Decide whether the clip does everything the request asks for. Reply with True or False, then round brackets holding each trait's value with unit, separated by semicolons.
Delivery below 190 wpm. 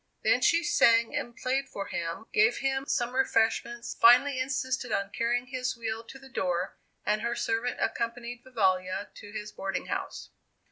True (160 wpm)